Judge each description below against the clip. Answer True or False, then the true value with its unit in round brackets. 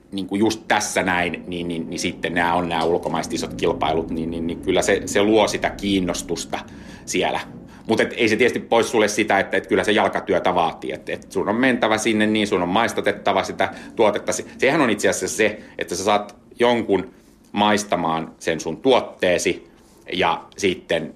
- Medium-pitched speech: False (100 Hz)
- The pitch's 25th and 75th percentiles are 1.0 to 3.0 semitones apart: False (3.9 semitones)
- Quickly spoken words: True (185 wpm)